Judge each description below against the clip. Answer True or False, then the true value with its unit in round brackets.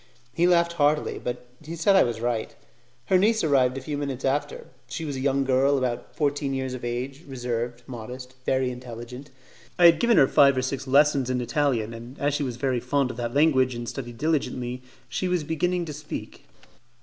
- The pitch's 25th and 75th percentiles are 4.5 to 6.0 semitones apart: False (3.0 semitones)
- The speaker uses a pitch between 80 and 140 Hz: True (135 Hz)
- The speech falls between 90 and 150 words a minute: False (205 wpm)